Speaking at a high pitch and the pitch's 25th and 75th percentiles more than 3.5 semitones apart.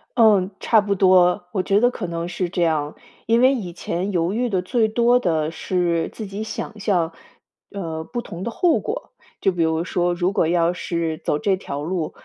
No: medium, 180 Hz; average, 4.0 semitones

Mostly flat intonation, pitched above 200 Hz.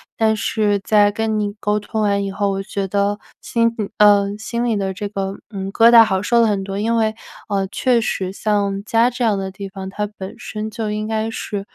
Yes: narrow, 1.8 semitones; high, 210 Hz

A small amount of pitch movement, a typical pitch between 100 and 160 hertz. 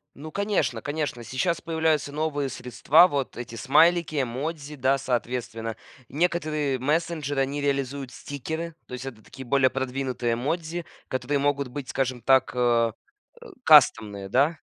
No: average, 3.5 semitones; medium, 140 Hz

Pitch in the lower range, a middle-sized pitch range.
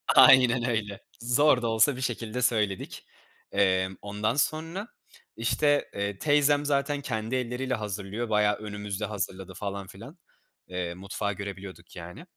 Yes: low, 110 Hz; average, 4.4 semitones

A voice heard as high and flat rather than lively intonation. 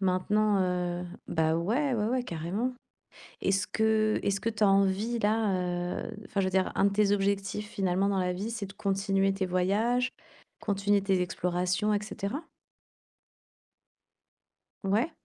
Yes: high, 200 Hz; narrow, 2.3 semitones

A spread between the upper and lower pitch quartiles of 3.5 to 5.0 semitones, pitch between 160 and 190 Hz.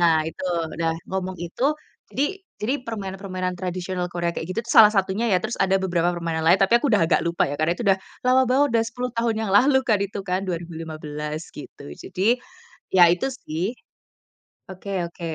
Yes: average, 3.8 semitones; medium, 185 Hz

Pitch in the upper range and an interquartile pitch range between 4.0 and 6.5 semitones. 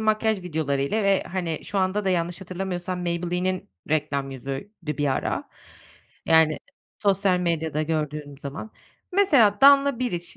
No: medium, 180 Hz; average, 4.4 semitones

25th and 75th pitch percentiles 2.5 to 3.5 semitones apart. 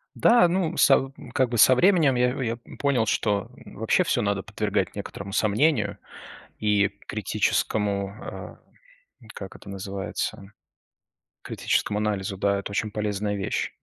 No: average, 4.1 semitones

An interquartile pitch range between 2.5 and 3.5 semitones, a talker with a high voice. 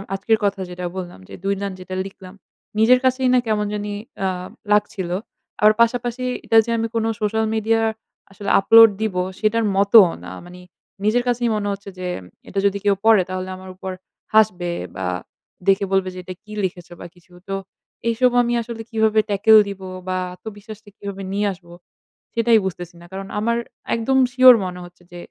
Yes: average, 3.1 semitones; high, 205 Hz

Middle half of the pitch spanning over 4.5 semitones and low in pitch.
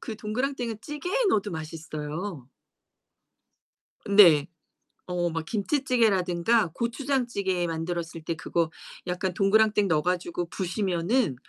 No: average, 5.1 semitones; high, 190 Hz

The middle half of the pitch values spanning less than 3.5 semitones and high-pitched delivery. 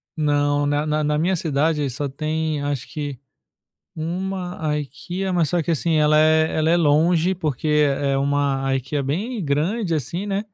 No: average, 2.9 semitones; medium, 155 Hz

